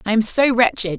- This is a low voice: No, high, 225 Hz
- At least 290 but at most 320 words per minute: No, fast, 245 wpm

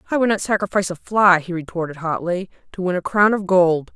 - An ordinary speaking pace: No, fast, 230 wpm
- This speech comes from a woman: Yes, female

